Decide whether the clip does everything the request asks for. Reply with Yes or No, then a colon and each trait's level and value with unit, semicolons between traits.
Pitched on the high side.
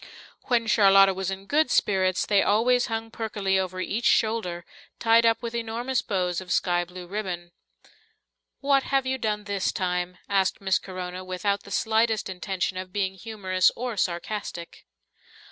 Yes: high, 200 Hz